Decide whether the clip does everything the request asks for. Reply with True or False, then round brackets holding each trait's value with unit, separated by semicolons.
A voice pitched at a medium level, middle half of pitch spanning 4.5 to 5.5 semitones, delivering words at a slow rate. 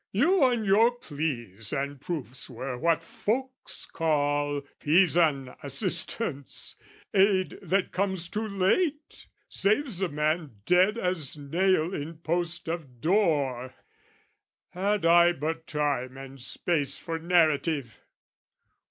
True (165 Hz; 4.9 semitones; 110 wpm)